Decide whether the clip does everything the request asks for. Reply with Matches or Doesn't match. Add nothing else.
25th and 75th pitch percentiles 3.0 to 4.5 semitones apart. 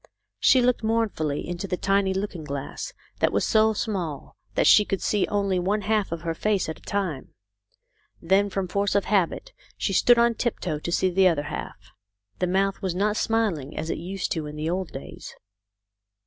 Matches